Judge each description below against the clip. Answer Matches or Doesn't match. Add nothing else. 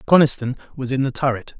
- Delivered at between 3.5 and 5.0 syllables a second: Doesn't match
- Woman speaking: Doesn't match